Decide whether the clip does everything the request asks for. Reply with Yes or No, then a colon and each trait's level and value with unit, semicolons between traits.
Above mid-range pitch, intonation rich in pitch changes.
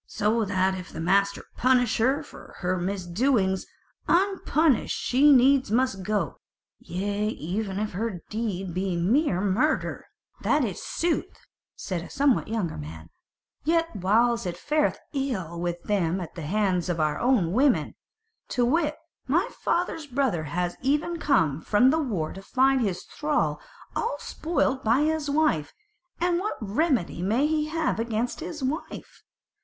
Yes: high, 225 Hz; wide, 7.5 semitones